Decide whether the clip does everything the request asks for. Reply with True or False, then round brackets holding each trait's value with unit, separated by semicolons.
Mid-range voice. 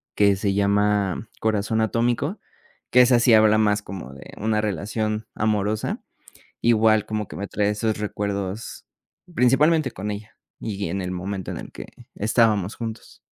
False (105 Hz)